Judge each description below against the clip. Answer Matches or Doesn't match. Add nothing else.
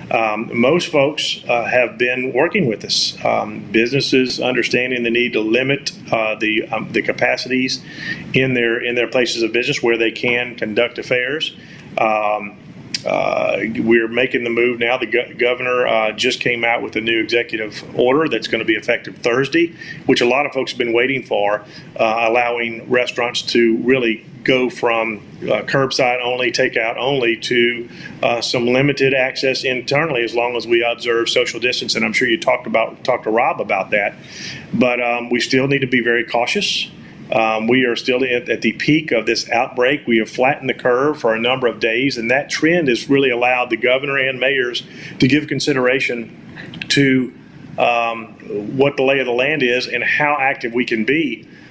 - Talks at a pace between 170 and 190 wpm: Matches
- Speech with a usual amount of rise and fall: Doesn't match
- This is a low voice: Matches